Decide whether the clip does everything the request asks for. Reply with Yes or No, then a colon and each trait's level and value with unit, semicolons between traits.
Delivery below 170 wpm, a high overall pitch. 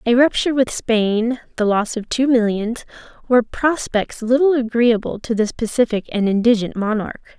Yes: average, 155 wpm; high, 230 Hz